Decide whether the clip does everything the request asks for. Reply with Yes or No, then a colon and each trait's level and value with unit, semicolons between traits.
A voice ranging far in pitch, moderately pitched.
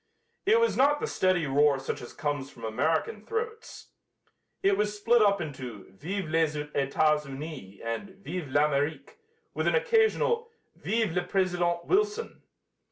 Yes: wide, 8.0 semitones; medium, 170 Hz